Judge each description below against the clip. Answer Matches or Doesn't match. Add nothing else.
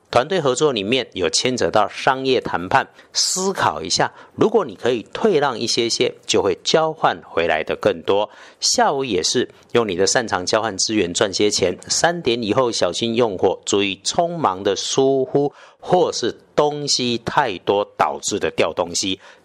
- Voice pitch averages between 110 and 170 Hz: Matches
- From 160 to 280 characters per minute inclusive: Matches